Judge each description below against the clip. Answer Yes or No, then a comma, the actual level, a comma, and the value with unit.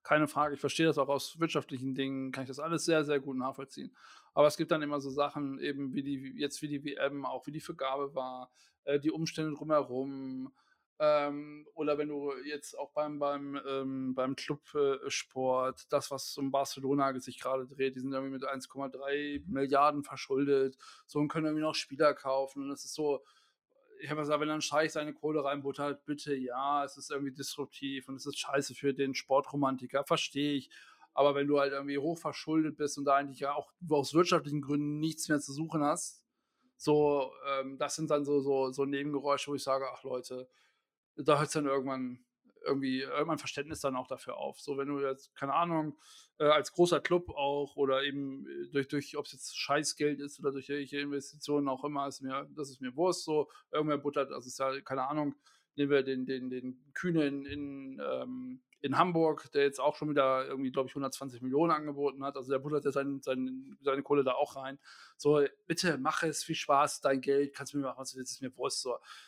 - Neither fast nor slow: No, fast, 205 wpm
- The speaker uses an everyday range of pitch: No, narrow, 1.7 semitones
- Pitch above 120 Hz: Yes, medium, 140 Hz